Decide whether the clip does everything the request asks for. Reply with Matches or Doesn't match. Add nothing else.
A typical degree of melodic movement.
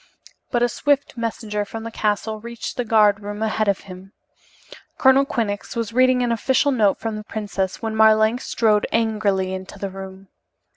Doesn't match